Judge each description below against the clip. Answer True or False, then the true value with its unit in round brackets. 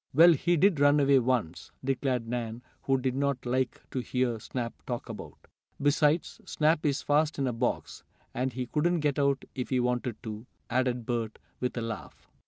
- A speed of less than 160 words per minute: False (185 wpm)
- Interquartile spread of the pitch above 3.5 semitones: False (2.9 semitones)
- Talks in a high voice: False (130 Hz)